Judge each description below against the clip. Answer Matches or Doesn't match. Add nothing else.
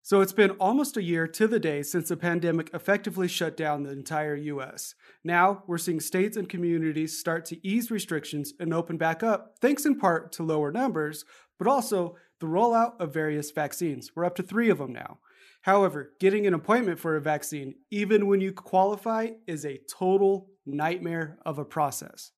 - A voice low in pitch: Doesn't match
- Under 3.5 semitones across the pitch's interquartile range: Doesn't match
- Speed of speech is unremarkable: Matches